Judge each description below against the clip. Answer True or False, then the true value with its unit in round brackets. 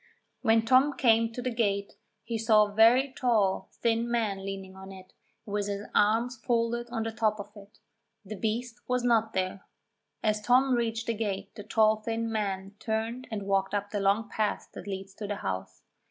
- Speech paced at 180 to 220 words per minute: True (190 wpm)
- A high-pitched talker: True (220 Hz)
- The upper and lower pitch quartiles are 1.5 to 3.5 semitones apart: True (2.5 semitones)